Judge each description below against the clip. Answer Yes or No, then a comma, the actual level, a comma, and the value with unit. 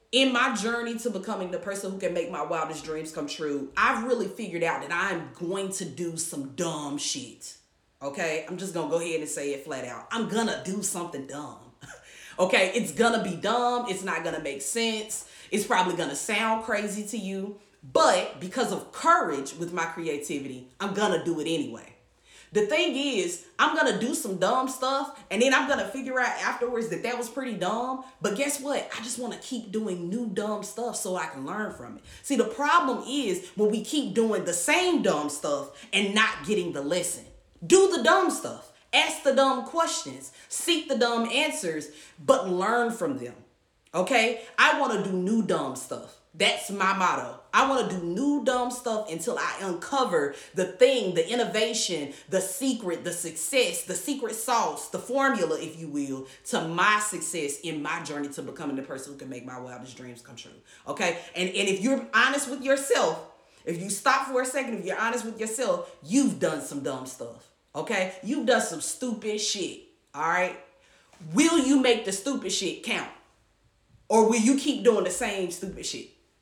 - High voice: Yes, high, 210 Hz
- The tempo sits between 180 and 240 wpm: Yes, average, 190 wpm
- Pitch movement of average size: No, wide, 6.8 semitones